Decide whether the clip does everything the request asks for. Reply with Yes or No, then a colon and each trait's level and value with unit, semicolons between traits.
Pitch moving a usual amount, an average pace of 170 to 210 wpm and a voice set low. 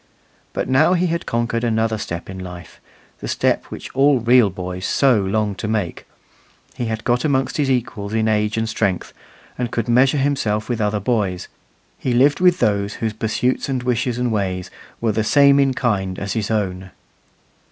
Yes: average, 3.7 semitones; average, 185 wpm; low, 110 Hz